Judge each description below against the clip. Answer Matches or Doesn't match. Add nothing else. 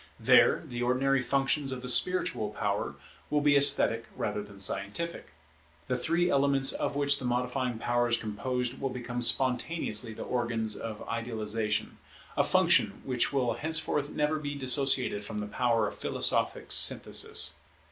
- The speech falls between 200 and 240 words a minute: Doesn't match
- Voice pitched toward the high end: Doesn't match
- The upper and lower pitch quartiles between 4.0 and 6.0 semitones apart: Doesn't match